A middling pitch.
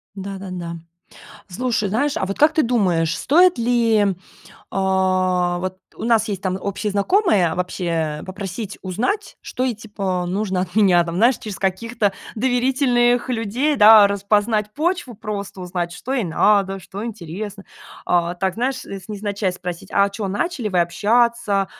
No: high, 200 Hz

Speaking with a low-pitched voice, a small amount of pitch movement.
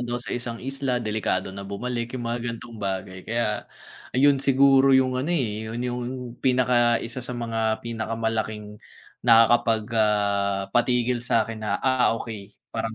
Yes: low, 115 Hz; narrow, 2.3 semitones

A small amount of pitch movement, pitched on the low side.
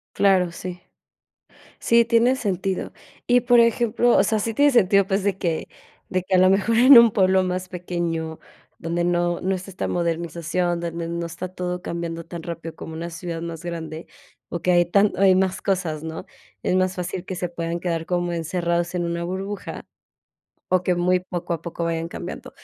No: narrow, 2.1 semitones; medium, 180 Hz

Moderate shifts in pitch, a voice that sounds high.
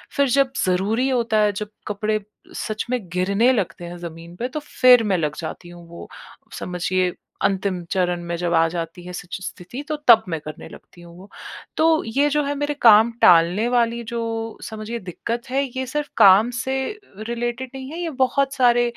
No: wide, 5.9 semitones; high, 215 Hz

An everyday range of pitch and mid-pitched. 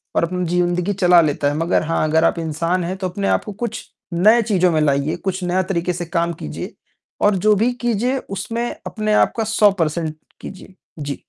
Yes: average, 3.5 semitones; medium, 180 Hz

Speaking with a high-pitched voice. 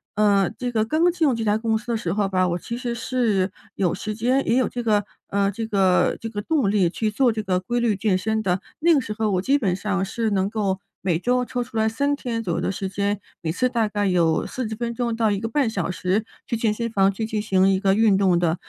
Yes: high, 215 Hz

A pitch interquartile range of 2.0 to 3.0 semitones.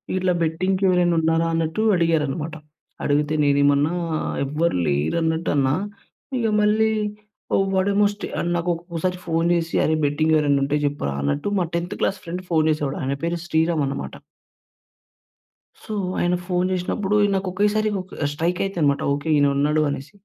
No: average, 3.7 semitones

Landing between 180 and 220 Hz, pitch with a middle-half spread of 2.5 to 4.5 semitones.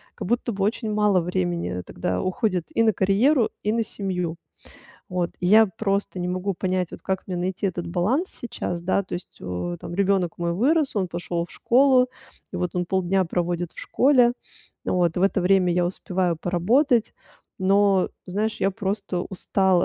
Yes: high, 190 Hz; average, 3.1 semitones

